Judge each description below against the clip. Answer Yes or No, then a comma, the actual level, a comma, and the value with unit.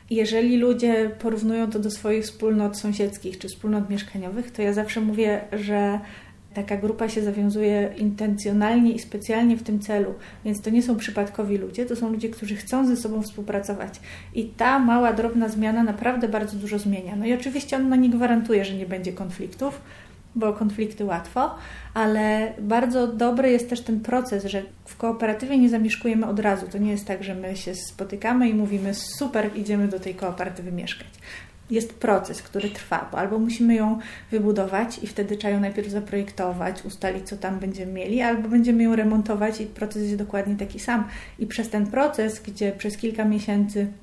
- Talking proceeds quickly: Yes, fast, 180 wpm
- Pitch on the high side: Yes, high, 215 Hz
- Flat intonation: Yes, narrow, 2.0 semitones